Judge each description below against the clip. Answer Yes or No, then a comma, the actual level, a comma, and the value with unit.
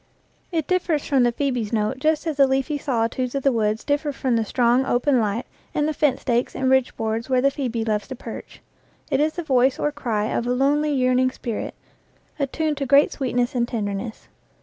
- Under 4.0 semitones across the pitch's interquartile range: Yes, average, 3.4 semitones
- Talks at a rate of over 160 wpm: Yes, fast, 205 wpm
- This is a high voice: Yes, very high, 260 Hz